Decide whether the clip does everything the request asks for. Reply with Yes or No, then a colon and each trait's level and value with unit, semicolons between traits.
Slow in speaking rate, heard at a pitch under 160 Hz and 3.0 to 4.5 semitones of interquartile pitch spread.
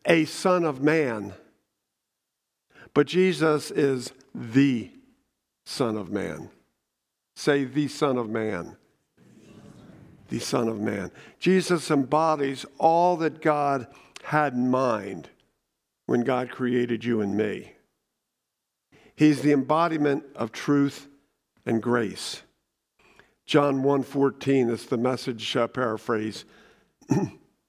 Yes: slow, 110 wpm; medium, 140 Hz; average, 3.9 semitones